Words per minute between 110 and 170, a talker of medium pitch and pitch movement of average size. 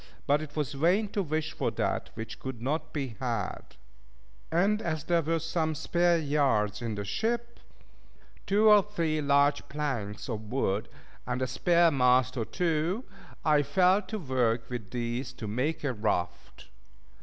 No: average, 160 wpm; medium, 145 Hz; wide, 5.7 semitones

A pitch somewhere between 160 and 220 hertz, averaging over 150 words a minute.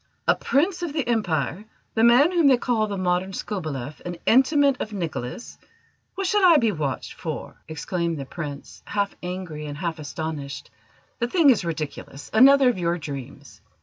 Yes: medium, 185 Hz; average, 170 wpm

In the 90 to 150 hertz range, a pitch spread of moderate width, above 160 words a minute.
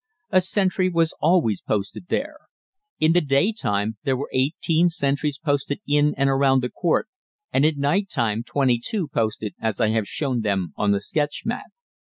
No: medium, 140 Hz; wide, 6.4 semitones; average, 180 wpm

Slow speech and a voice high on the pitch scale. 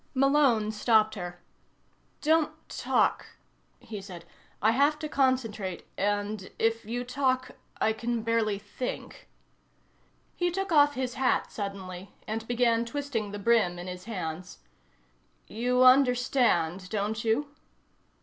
Yes: slow, 120 wpm; high, 225 Hz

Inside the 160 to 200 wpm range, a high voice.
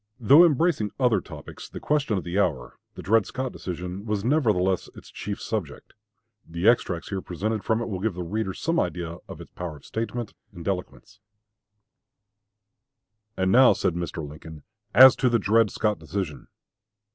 No: average, 170 wpm; low, 100 Hz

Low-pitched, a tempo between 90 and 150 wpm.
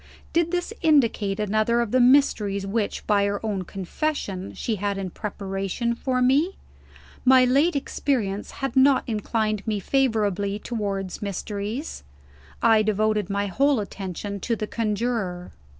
No: high, 215 Hz; slow, 135 wpm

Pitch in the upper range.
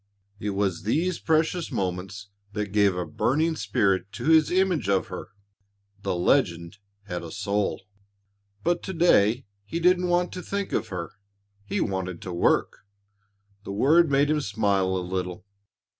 No: low, 105 Hz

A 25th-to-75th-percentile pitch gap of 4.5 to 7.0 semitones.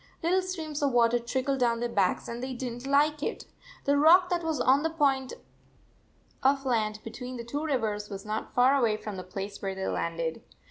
Yes: average, 4.8 semitones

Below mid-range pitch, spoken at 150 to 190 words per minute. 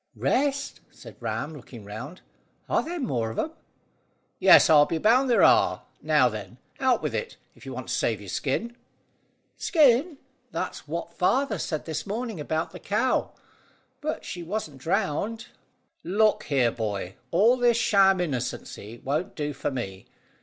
No: medium, 175 Hz; average, 160 wpm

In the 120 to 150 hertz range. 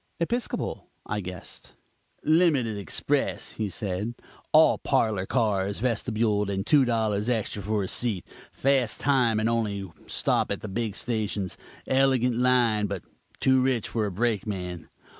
No: low, 110 Hz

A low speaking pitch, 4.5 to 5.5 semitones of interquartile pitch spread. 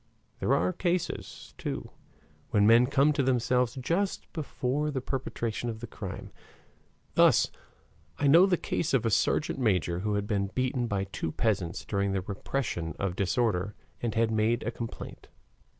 Yes: low, 115 Hz; average, 5.1 semitones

